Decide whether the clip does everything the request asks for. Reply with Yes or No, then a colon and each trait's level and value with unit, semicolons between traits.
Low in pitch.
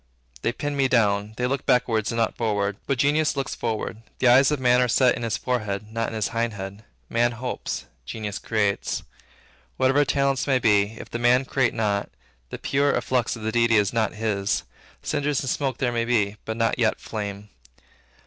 Yes: low, 115 Hz